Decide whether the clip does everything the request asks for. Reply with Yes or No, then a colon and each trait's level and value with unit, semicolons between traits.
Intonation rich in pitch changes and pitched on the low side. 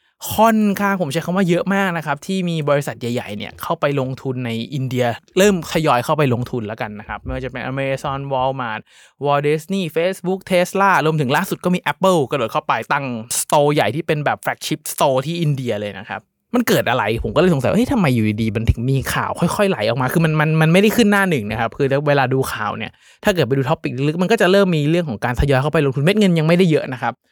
No: wide, 5.7 semitones; medium, 150 Hz